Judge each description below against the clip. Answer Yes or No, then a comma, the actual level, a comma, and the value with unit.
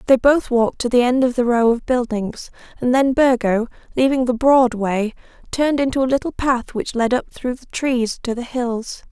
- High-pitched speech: Yes, high, 245 Hz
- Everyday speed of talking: No, fast, 210 wpm